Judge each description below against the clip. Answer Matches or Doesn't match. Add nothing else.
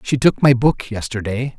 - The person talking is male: Matches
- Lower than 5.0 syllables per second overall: Matches